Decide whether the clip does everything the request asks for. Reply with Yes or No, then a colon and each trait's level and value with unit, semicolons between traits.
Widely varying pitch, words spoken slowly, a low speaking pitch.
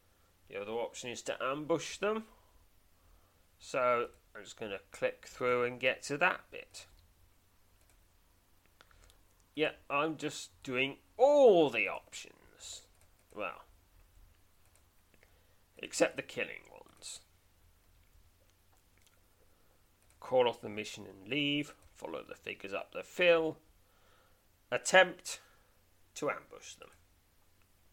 Yes: wide, 8.5 semitones; slow, 100 wpm; very low, 90 Hz